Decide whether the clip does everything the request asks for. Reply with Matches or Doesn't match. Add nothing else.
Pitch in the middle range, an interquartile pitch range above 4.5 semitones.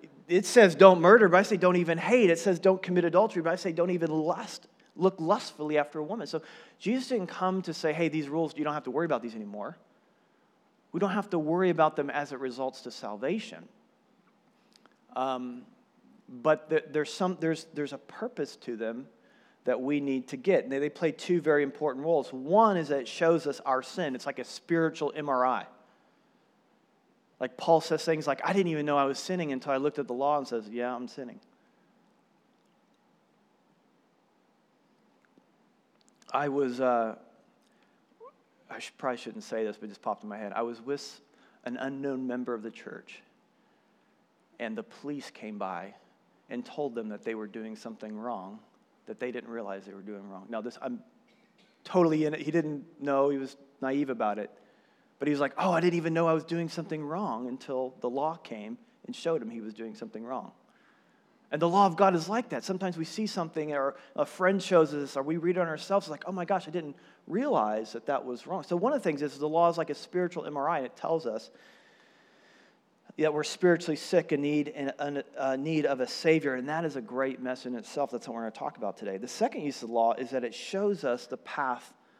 Matches